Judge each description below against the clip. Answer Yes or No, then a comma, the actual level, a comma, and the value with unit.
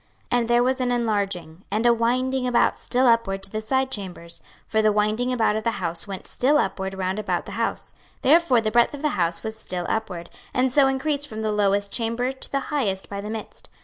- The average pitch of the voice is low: No, high, 220 Hz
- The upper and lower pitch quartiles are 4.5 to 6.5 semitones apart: No, average, 4.1 semitones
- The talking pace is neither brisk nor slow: No, fast, 225 wpm